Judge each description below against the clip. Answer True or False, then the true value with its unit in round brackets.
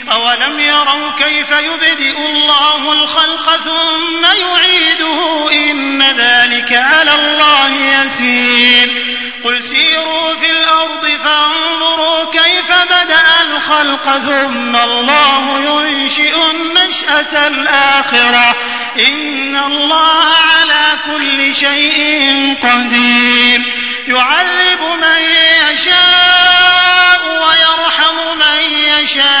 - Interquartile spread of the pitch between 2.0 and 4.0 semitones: True (2.8 semitones)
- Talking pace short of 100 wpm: True (80 wpm)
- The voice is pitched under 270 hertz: False (300 Hz)